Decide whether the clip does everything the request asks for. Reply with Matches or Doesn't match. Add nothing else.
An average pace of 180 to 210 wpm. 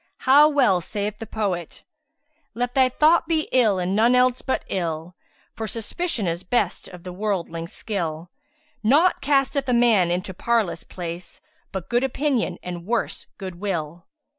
Doesn't match